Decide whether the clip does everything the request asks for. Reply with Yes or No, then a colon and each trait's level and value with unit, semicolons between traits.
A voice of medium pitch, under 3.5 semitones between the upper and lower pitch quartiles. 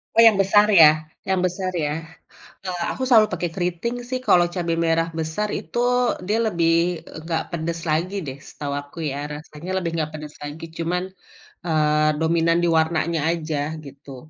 Yes: medium, 165 Hz; average, 2.8 semitones